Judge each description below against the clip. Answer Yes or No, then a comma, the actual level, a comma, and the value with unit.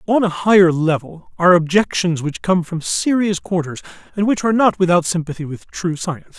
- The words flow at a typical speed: Yes, average, 190 wpm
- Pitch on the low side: No, medium, 180 Hz